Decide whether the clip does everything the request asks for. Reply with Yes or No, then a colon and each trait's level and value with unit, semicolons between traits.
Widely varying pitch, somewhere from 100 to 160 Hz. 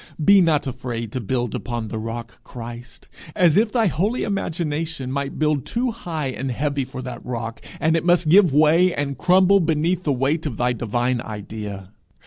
Yes: wide, 5.9 semitones; medium, 140 Hz